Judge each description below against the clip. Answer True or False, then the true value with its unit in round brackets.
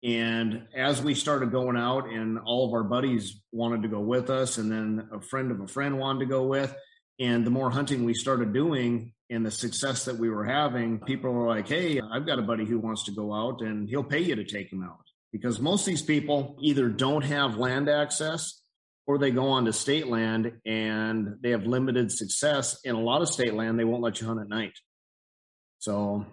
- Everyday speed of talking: False (225 wpm)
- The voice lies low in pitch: True (120 Hz)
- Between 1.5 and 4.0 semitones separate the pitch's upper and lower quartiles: True (3.4 semitones)